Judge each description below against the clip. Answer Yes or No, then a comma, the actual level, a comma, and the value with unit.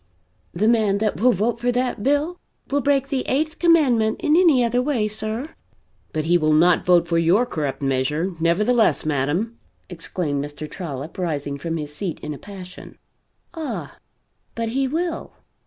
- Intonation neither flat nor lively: No, wide, 7.6 semitones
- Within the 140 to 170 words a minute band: Yes, average, 165 wpm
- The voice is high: Yes, high, 205 Hz